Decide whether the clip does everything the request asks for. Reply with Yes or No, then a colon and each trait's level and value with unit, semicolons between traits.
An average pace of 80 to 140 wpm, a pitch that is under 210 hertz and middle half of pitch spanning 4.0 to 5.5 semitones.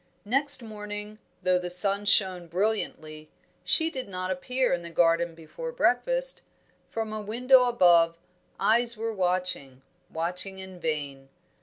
Yes: slow, 135 wpm; high, 190 Hz; average, 4.9 semitones